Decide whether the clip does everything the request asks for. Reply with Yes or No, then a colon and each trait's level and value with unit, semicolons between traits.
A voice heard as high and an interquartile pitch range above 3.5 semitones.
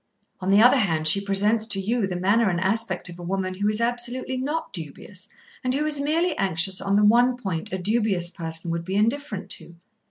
Yes: high, 200 Hz; average, 4.5 semitones